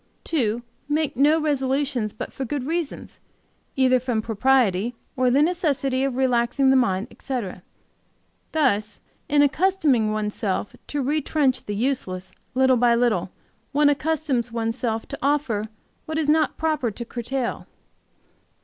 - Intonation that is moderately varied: Yes, average, 4.1 semitones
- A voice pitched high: Yes, very high, 260 Hz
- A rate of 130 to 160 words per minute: Yes, average, 140 wpm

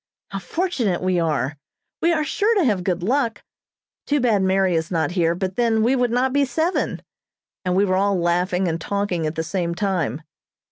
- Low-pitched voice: No, high, 190 Hz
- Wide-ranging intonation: Yes, wide, 5.9 semitones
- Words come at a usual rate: Yes, average, 195 wpm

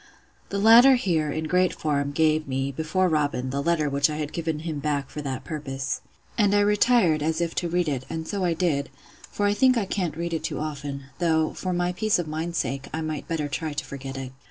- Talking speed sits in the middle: No, fast, 230 wpm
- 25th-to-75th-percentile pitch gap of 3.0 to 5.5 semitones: Yes, average, 3.7 semitones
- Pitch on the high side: No, medium, 155 Hz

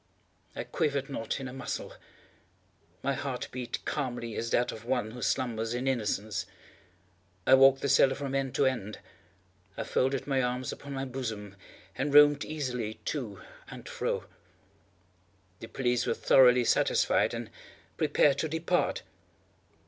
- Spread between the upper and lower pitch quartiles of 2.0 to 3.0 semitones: Yes, narrow, 2.6 semitones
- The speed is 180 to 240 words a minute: No, average, 145 wpm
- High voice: No, low, 130 Hz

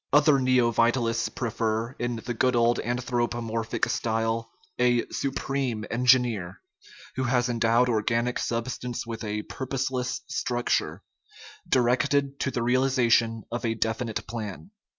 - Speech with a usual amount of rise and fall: No, narrow, 1.8 semitones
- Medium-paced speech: No, slow, 115 wpm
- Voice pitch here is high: No, low, 120 Hz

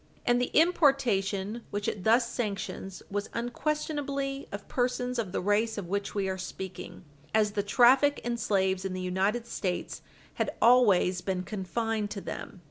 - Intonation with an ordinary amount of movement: Yes, average, 4.2 semitones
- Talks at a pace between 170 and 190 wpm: No, average, 160 wpm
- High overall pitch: Yes, high, 210 Hz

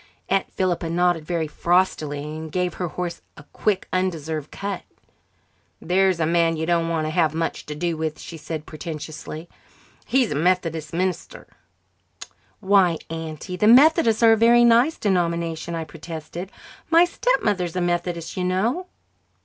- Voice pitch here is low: No, medium, 175 Hz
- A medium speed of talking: Yes, average, 155 wpm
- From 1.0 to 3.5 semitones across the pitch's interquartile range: Yes, average, 2.9 semitones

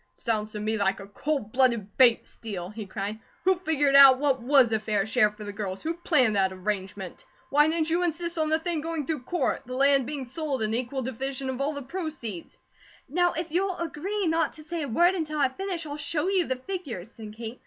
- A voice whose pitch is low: No, very high, 270 Hz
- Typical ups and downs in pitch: No, wide, 6.6 semitones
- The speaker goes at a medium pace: No, fast, 225 wpm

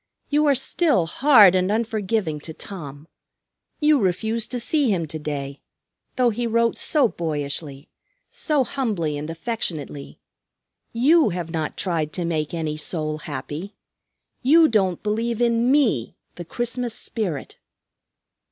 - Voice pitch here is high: Yes, high, 195 Hz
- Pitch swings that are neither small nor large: No, wide, 7.3 semitones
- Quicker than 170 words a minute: No, slow, 135 wpm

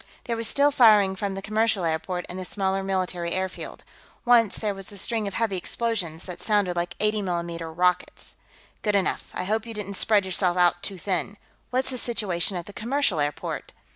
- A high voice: Yes, high, 195 Hz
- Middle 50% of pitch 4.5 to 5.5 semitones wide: No, average, 3.3 semitones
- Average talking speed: Yes, average, 195 wpm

